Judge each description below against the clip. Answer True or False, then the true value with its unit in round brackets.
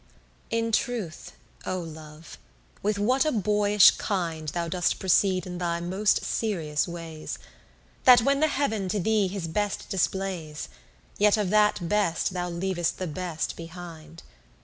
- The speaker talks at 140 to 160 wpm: True (150 wpm)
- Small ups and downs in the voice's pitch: False (3.8 semitones)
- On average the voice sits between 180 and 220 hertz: True (185 Hz)